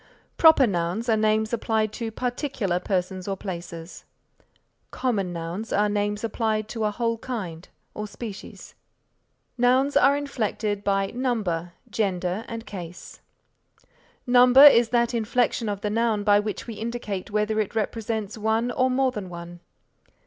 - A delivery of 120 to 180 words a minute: Yes, average, 140 wpm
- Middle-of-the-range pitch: No, high, 215 Hz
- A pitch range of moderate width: Yes, average, 3.1 semitones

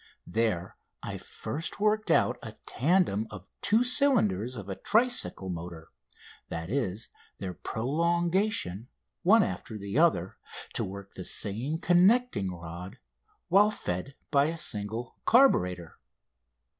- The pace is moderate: No, slow, 120 wpm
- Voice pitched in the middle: No, low, 115 Hz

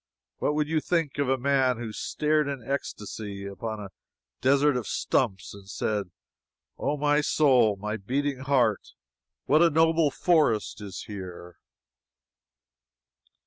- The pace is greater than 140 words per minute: No, slow, 135 wpm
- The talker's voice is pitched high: No, low, 130 Hz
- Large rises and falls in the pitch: Yes, wide, 5.8 semitones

